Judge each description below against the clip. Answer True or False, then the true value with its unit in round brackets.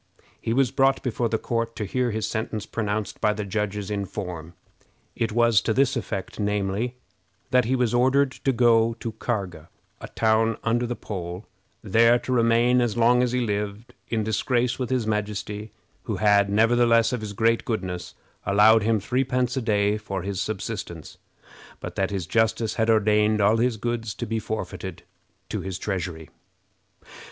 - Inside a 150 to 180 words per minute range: True (170 wpm)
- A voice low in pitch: True (110 Hz)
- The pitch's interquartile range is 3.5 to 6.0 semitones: False (2.6 semitones)